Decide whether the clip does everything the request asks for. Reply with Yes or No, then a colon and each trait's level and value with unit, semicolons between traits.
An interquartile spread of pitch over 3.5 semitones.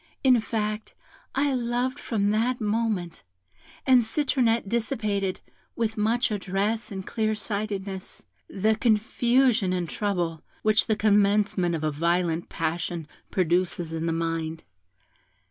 Yes: average, 4.2 semitones